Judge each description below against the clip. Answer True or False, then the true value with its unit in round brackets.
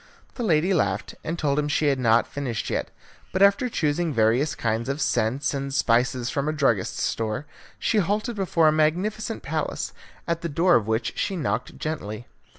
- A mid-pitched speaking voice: True (150 Hz)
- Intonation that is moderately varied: False (6.3 semitones)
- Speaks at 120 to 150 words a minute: False (180 wpm)